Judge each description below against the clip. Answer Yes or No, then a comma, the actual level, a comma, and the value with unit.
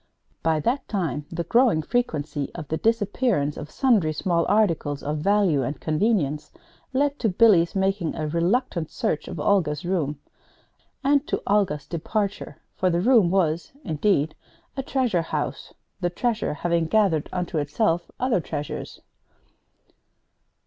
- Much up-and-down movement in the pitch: Yes, wide, 5.7 semitones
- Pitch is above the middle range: No, medium, 175 Hz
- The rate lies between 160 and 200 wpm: No, slow, 135 wpm